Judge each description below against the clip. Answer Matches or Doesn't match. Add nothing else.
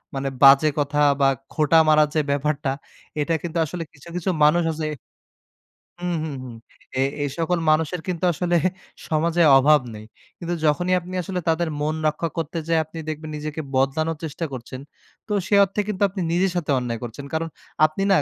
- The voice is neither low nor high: Matches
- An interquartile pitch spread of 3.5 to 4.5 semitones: Doesn't match